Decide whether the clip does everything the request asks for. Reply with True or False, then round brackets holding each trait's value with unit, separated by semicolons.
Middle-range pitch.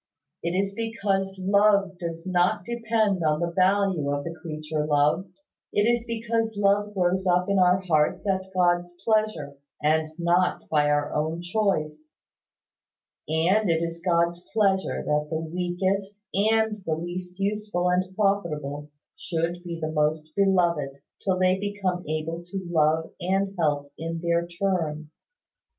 True (175 Hz)